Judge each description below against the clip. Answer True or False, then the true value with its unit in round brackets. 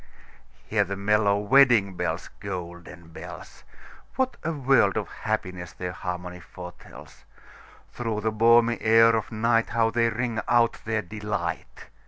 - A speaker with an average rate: False (115 wpm)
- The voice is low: True (110 Hz)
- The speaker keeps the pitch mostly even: False (4.3 semitones)